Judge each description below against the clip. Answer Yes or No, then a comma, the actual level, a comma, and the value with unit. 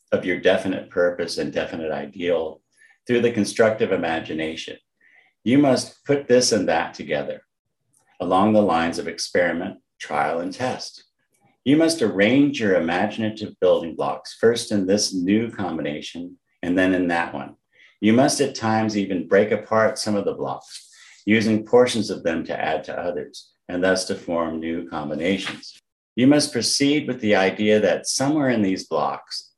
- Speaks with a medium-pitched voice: No, low, 110 Hz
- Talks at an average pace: Yes, average, 160 wpm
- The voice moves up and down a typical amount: No, wide, 7.0 semitones